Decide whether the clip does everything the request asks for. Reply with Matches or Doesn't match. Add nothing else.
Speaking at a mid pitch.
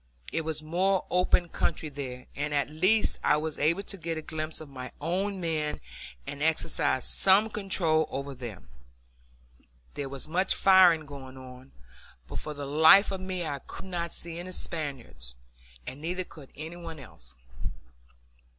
Matches